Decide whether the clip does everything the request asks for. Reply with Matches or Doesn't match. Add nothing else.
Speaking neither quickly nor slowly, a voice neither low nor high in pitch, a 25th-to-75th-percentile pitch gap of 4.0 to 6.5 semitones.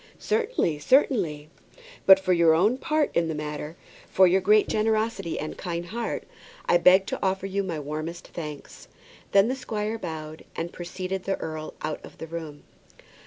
Matches